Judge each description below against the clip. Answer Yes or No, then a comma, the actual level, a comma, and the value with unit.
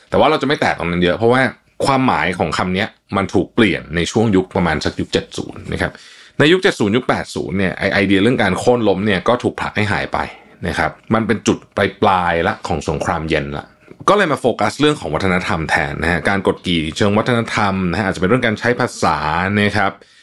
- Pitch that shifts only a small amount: No, average, 3.9 semitones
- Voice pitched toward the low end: Yes, very low, 95 Hz